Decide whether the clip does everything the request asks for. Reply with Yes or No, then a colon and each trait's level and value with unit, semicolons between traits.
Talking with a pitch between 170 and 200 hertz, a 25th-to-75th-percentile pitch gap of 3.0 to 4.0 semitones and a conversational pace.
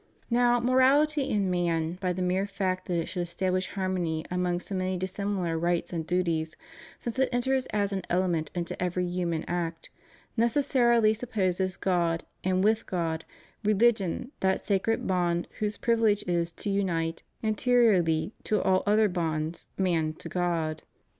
Yes: medium, 185 Hz; average, 3.7 semitones; average, 150 wpm